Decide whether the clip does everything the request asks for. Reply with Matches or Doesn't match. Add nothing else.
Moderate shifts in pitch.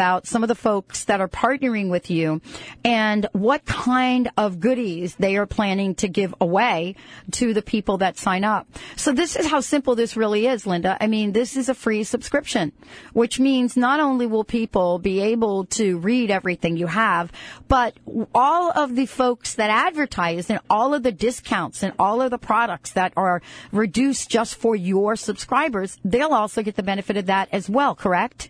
Matches